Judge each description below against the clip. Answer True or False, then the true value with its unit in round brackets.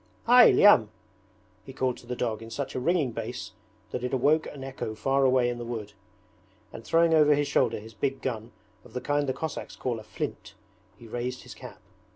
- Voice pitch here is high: False (125 Hz)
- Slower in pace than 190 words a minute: False (205 wpm)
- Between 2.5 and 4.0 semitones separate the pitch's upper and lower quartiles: True (3.5 semitones)